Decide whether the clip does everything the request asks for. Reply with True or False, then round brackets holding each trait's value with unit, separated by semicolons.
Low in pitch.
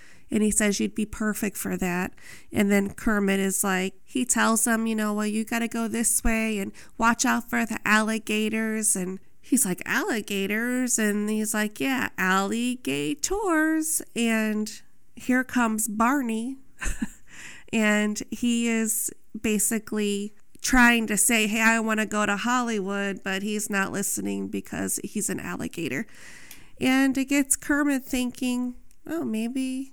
False (220 Hz)